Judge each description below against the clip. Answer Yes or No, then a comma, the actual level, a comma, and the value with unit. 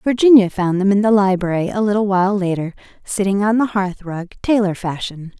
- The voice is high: Yes, high, 195 Hz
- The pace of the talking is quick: No, average, 190 wpm